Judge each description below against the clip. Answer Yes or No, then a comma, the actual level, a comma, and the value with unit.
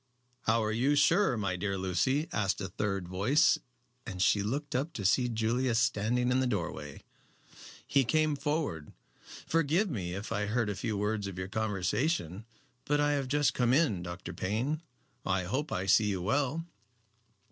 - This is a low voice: Yes, low, 110 Hz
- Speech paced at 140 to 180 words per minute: Yes, average, 170 wpm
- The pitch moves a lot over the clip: Yes, wide, 6.3 semitones